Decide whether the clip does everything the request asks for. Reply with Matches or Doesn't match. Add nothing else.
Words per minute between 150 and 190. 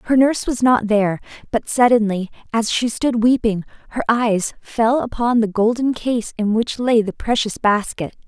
Matches